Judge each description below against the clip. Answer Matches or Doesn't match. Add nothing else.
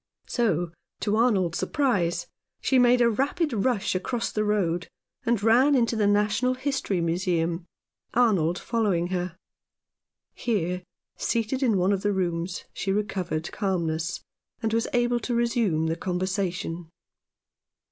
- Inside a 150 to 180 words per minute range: Doesn't match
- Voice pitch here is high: Matches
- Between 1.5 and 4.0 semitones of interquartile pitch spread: Doesn't match